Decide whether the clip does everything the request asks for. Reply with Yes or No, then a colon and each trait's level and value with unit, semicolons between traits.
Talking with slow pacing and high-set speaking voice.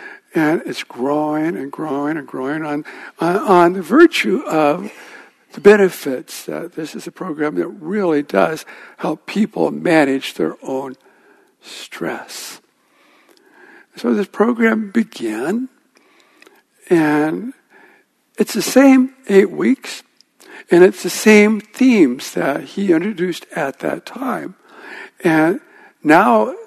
Yes: slow, 115 wpm; high, 210 Hz